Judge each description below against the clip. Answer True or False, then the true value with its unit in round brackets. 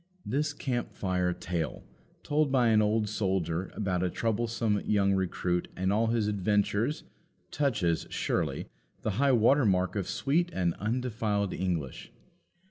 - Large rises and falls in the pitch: False (4.1 semitones)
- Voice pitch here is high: False (105 Hz)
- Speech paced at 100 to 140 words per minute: True (135 wpm)